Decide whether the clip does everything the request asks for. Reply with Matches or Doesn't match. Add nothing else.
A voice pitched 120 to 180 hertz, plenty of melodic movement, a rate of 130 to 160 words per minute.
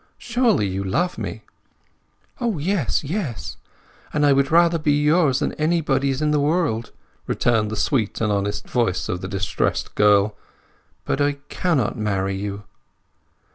Matches